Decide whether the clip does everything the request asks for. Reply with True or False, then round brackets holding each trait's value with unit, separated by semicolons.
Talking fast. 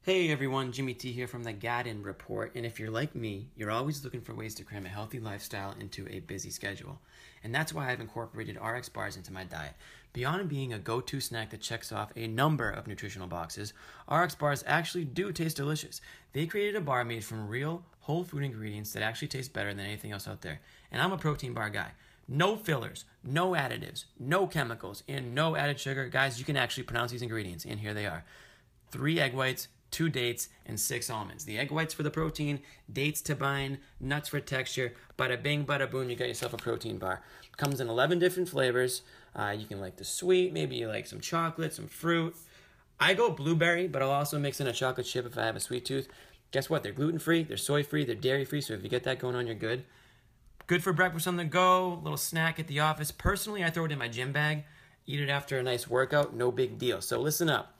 True (230 wpm)